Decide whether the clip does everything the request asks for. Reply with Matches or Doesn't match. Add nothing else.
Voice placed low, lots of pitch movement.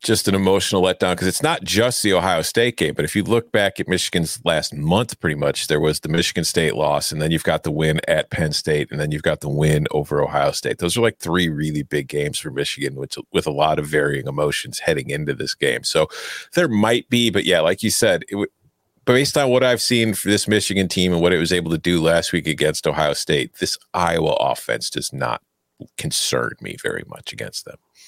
Matches